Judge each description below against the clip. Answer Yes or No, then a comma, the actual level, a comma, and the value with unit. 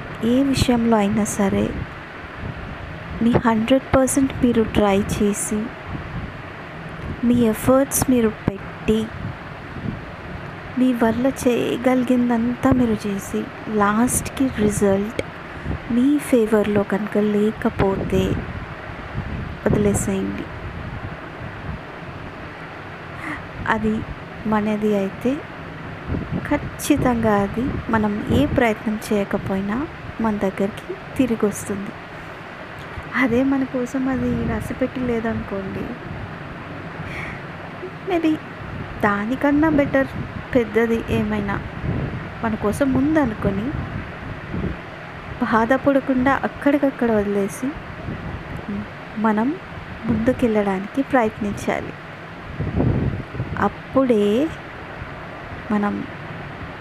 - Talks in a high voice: Yes, high, 225 Hz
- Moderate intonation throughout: Yes, average, 3.8 semitones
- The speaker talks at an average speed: No, slow, 65 wpm